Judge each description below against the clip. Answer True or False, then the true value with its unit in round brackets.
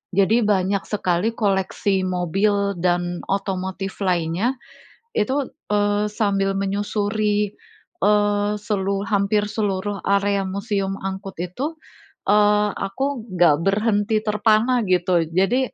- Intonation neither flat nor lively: False (1.6 semitones)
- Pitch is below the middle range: False (200 Hz)